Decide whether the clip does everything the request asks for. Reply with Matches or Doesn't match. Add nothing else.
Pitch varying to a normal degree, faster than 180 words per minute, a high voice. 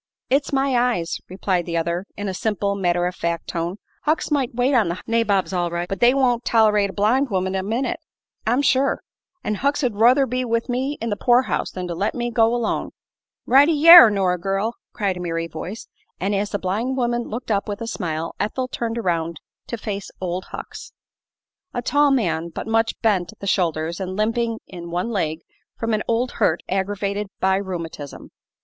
Matches